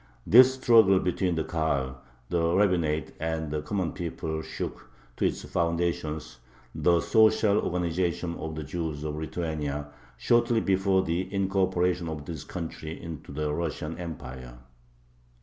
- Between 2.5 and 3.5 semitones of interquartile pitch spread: Yes, average, 3.2 semitones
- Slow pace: Yes, slow, 130 wpm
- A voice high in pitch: No, very low, 85 Hz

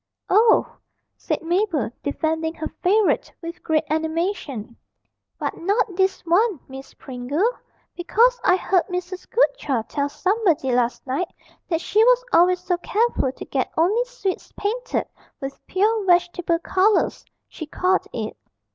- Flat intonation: No, average, 4.8 semitones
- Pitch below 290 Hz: No, very high, 355 Hz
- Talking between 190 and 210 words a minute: No, slow, 135 wpm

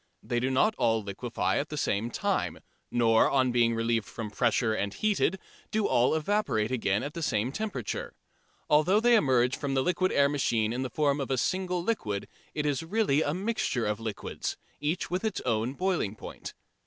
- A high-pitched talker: No, low, 135 Hz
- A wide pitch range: Yes, wide, 7.3 semitones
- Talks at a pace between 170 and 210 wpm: Yes, average, 190 wpm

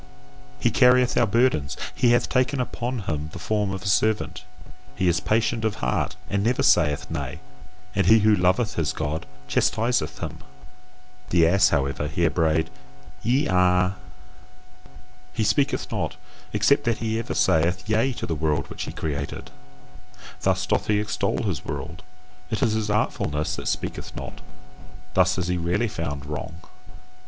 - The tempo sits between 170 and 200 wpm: No, average, 160 wpm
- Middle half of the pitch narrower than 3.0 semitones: No, wide, 5.4 semitones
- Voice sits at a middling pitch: No, very low, 95 Hz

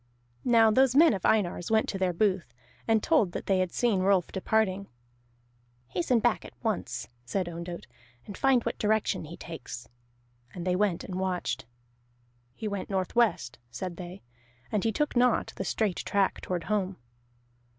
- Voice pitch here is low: No, high, 195 Hz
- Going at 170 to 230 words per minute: No, average, 160 wpm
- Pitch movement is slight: No, average, 3.6 semitones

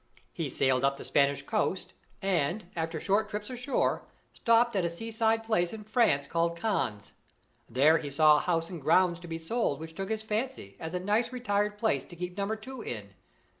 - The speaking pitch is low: No, medium, 180 Hz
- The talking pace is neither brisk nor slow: Yes, average, 195 wpm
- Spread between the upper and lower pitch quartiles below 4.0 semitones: No, wide, 5.4 semitones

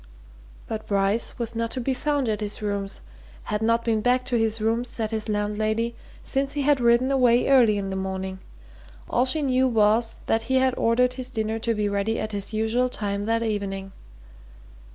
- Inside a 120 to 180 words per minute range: No, average, 195 wpm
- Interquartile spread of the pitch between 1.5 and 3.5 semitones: Yes, average, 3.0 semitones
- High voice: Yes, high, 225 Hz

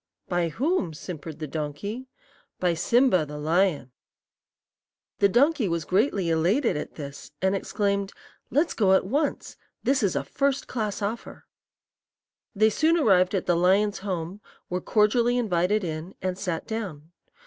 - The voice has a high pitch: Yes, high, 195 Hz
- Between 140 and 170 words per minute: Yes, average, 145 wpm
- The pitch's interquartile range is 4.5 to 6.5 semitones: Yes, average, 5.0 semitones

